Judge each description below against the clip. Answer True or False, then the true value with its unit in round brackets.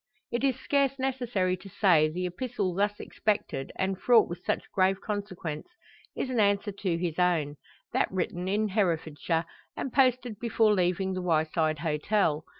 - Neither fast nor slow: True (155 wpm)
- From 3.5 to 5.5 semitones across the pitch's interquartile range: True (4.1 semitones)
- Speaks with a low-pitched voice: False (190 Hz)